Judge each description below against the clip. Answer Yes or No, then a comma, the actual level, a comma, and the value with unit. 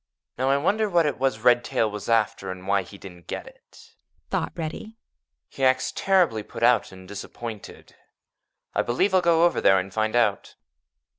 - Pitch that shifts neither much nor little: No, wide, 8.3 semitones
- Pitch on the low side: Yes, low, 120 Hz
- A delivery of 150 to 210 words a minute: Yes, average, 175 wpm